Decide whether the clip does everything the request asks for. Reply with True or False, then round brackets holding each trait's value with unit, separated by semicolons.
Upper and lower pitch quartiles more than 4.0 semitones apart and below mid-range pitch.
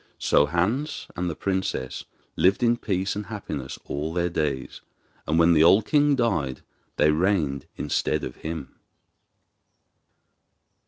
True (5.1 semitones; 85 Hz)